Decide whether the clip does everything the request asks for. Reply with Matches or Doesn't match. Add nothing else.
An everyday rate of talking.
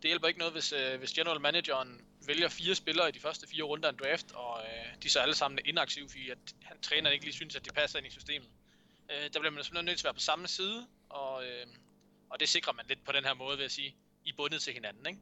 Doesn't match